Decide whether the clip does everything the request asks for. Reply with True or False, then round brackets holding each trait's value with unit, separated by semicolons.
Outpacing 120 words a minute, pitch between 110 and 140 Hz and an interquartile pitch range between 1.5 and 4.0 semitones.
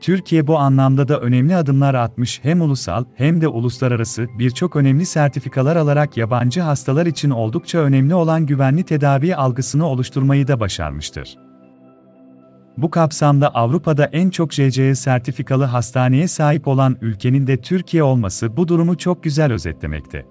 False (140 wpm; 135 Hz; 4.4 semitones)